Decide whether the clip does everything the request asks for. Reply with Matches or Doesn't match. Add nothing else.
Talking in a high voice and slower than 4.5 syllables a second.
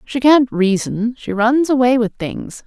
Matches